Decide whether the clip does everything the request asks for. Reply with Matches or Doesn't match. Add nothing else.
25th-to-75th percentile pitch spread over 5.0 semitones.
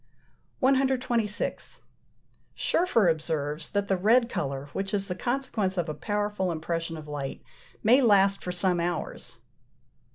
Matches